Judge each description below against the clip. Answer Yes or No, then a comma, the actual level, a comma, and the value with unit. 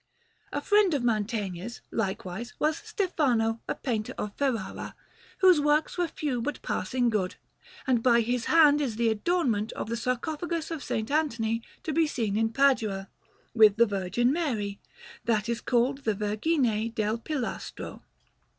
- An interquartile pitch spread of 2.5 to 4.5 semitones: No, average, 5.3 semitones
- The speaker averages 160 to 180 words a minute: No, average, 150 wpm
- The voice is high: Yes, high, 235 Hz